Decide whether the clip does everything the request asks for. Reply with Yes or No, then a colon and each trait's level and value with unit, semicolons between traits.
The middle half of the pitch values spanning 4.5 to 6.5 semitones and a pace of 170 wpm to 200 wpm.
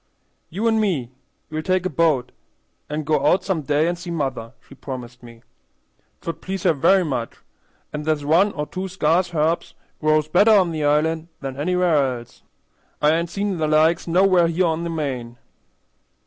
No: average, 3.5 semitones; average, 175 wpm